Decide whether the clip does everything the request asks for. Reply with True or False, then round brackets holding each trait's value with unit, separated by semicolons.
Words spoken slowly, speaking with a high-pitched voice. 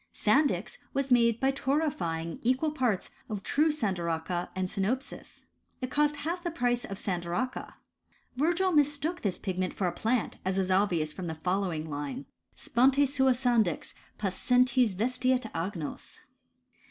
False (145 wpm; 230 Hz)